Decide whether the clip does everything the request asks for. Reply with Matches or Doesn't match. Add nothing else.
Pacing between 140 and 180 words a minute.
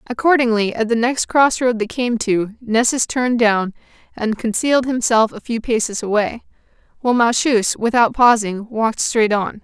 Matches